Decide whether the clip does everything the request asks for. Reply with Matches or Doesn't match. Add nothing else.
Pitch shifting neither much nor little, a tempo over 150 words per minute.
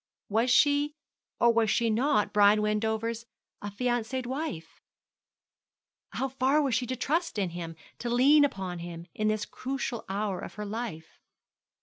Doesn't match